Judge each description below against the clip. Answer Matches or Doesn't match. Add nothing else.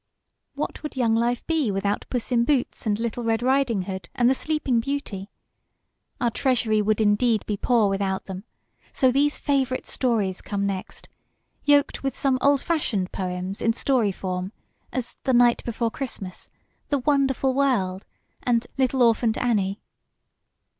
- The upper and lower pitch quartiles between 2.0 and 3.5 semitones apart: Doesn't match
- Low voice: Doesn't match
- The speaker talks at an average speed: Matches